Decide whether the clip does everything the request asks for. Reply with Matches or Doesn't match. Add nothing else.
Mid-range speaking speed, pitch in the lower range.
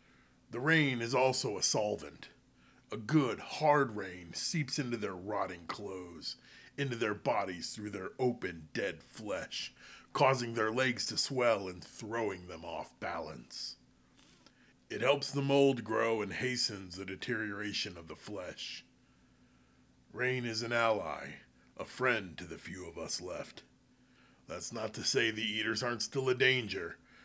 Matches